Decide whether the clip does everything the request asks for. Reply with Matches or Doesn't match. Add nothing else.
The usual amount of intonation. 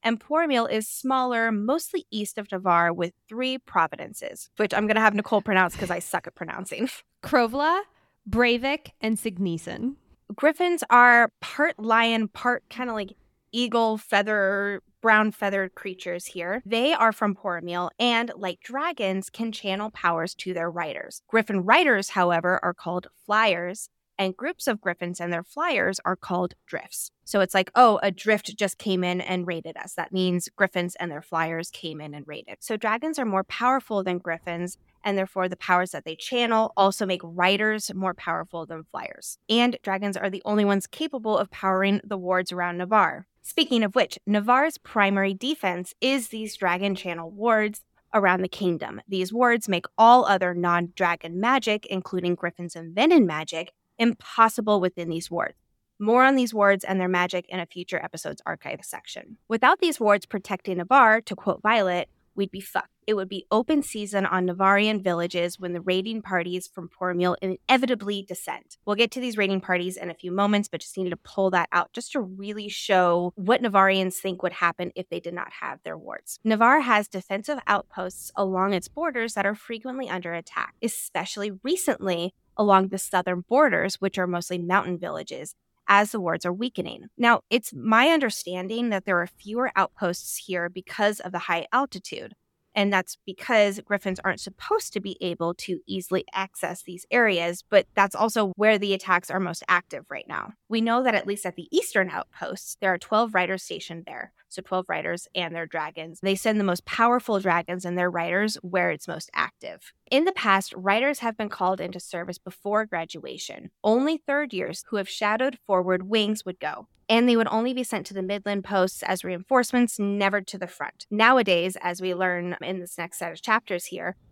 Matches